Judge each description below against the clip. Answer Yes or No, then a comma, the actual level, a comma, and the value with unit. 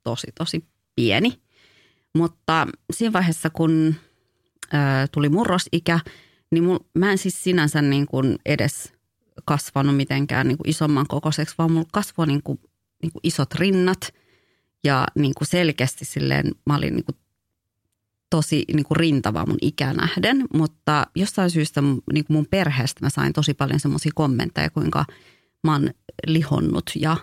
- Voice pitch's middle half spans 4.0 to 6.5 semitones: No, average, 2.9 semitones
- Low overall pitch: No, medium, 155 Hz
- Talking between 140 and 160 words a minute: Yes, average, 150 wpm